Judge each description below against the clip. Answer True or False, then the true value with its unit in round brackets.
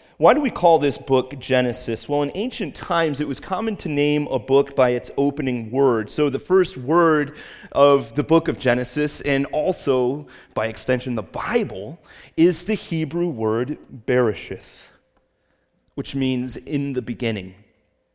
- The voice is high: False (140 Hz)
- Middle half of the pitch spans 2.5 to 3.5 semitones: False (4.0 semitones)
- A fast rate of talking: False (155 wpm)